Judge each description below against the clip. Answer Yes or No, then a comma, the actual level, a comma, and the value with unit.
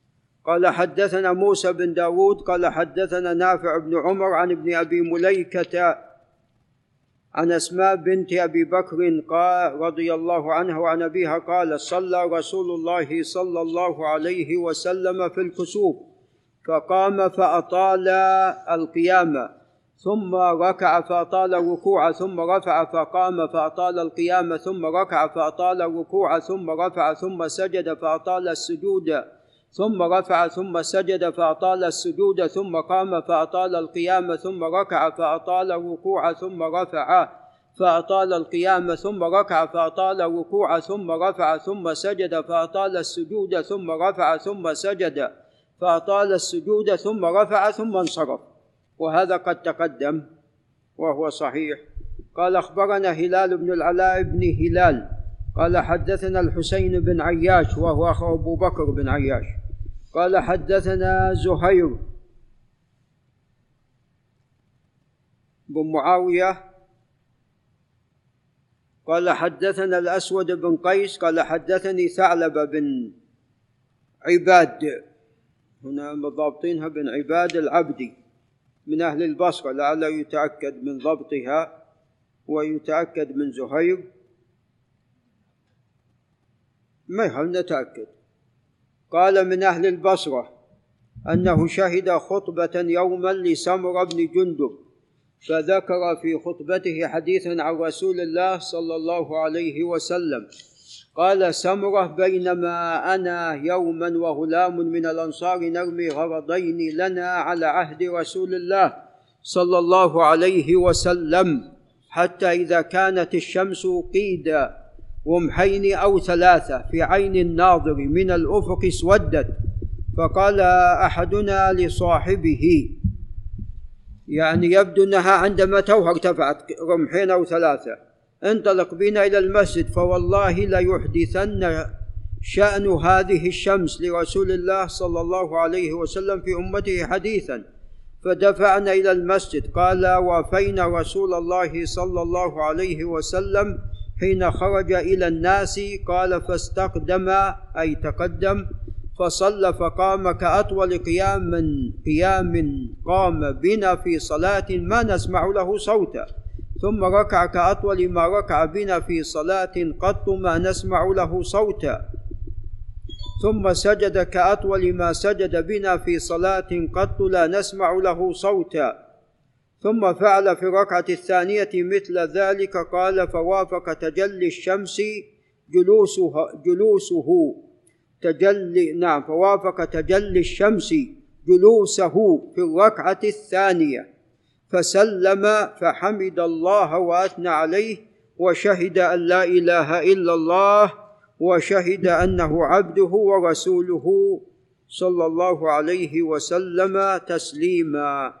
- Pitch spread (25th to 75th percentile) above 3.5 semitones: No, average, 2.9 semitones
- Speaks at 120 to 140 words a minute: No, average, 105 wpm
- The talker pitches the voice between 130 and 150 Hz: No, medium, 175 Hz